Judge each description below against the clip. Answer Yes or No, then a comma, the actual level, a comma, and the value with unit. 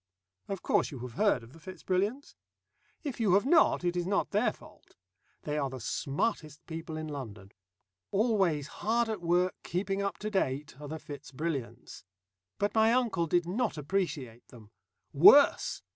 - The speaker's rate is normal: Yes, average, 170 wpm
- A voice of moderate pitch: Yes, medium, 175 Hz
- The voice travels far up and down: Yes, wide, 6.0 semitones